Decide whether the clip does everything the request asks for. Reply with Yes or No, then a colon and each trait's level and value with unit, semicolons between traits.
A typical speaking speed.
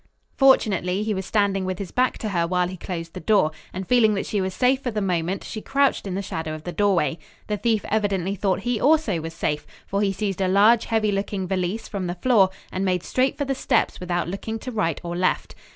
No: fast, 235 wpm